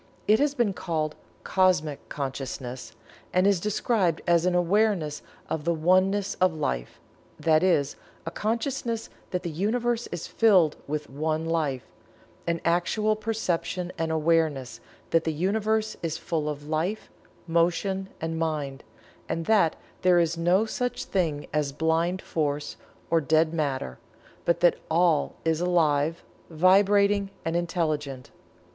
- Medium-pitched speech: Yes, medium, 170 Hz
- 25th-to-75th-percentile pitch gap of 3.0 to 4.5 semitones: Yes, average, 3.7 semitones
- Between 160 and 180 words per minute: No, slow, 135 wpm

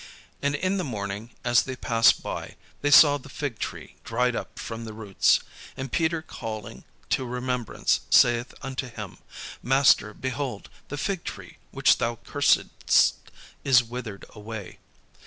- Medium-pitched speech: No, low, 125 Hz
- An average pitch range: Yes, average, 3.4 semitones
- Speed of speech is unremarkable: Yes, average, 145 wpm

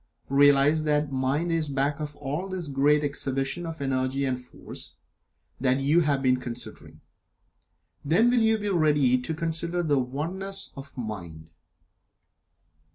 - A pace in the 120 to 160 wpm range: Yes, average, 140 wpm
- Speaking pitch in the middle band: Yes, medium, 145 Hz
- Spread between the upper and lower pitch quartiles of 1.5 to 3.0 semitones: No, average, 3.6 semitones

